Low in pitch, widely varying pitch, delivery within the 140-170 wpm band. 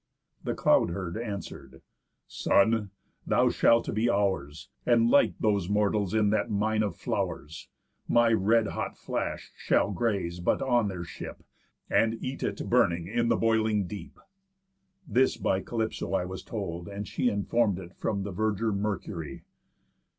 No: low, 105 Hz; average, 3.2 semitones; average, 150 wpm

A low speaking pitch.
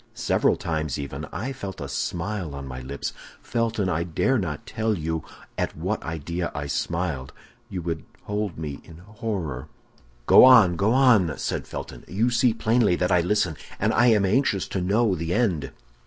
Yes: very low, 90 Hz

